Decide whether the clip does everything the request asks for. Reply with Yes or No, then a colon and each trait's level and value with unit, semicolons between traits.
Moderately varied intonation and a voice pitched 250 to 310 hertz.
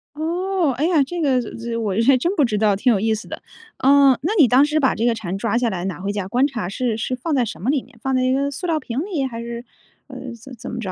Yes: average, 4.1 semitones; very high, 255 Hz